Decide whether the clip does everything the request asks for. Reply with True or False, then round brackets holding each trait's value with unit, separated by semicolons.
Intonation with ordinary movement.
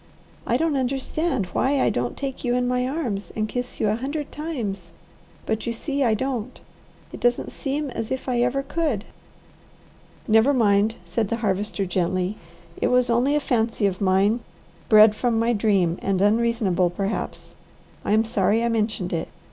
True (4.1 semitones)